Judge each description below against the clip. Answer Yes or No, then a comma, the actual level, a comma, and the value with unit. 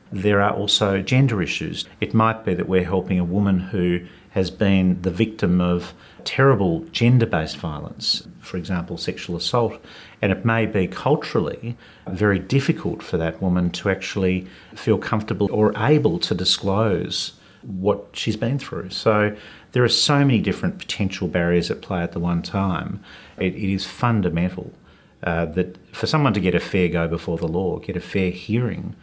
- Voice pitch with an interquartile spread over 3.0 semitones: Yes, average, 3.7 semitones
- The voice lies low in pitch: Yes, low, 100 Hz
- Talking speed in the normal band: Yes, average, 170 wpm